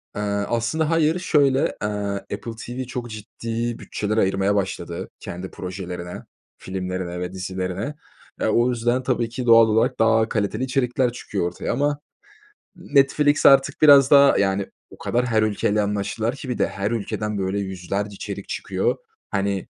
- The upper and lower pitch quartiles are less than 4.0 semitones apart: No, average, 4.6 semitones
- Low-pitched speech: Yes, low, 110 Hz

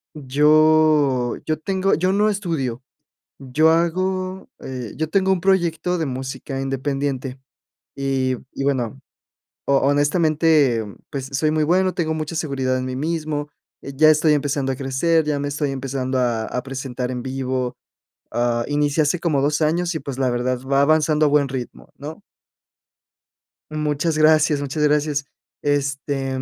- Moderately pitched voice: Yes, medium, 145 Hz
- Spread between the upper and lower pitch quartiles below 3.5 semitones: Yes, average, 3.0 semitones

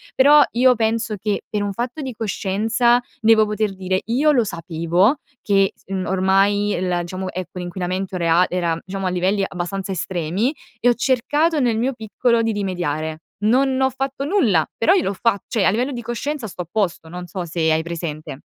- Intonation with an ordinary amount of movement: Yes, average, 4.9 semitones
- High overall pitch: Yes, high, 200 Hz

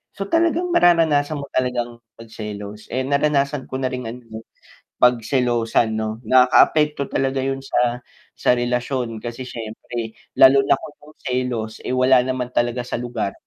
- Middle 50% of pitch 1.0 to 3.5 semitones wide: Yes, narrow, 2.5 semitones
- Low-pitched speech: Yes, low, 125 Hz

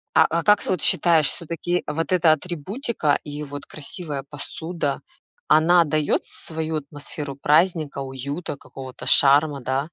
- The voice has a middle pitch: Yes, medium, 155 Hz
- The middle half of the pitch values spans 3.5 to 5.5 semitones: No, average, 3.0 semitones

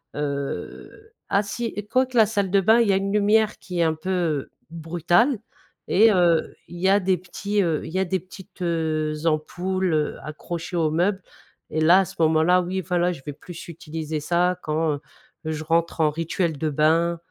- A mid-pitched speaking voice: Yes, medium, 175 Hz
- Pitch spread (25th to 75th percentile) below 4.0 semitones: Yes, average, 3.2 semitones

